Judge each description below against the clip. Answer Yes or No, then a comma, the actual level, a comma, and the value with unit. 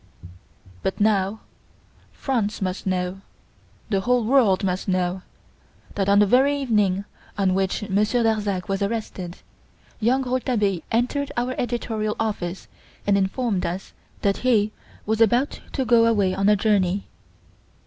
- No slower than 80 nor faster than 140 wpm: Yes, slow, 135 wpm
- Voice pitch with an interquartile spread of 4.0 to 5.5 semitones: No, average, 3.6 semitones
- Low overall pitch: No, high, 210 Hz